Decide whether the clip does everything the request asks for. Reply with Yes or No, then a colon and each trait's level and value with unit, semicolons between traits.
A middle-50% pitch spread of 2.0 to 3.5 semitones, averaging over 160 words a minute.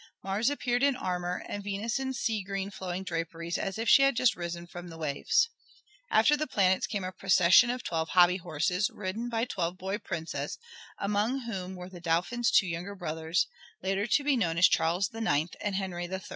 No: average, 4.3 semitones; average, 195 wpm